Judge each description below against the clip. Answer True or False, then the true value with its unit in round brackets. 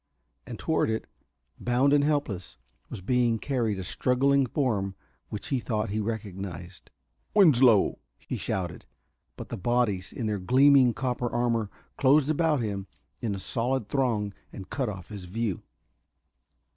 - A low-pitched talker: True (115 Hz)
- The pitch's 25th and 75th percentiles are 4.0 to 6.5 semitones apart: True (4.7 semitones)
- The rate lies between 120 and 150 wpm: True (145 wpm)